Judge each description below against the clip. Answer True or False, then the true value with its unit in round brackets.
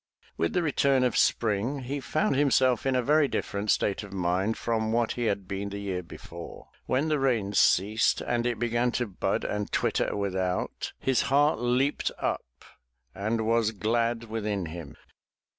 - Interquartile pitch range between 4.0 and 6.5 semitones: True (4.3 semitones)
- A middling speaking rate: True (170 wpm)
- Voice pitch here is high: False (115 Hz)